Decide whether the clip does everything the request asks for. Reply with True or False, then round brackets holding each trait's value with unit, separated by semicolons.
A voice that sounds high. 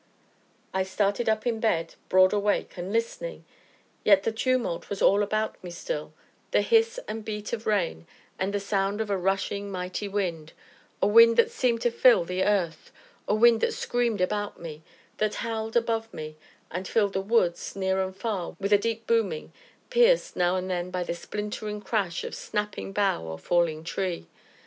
True (205 Hz)